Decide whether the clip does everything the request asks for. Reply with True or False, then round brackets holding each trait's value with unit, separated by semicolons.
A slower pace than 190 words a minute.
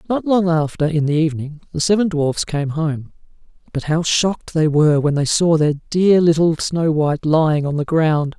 False (200 wpm)